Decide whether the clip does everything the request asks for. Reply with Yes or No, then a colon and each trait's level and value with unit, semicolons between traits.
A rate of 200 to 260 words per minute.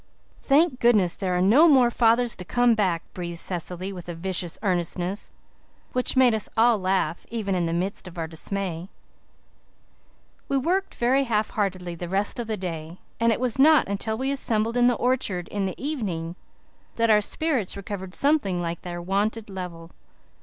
No: average, 175 wpm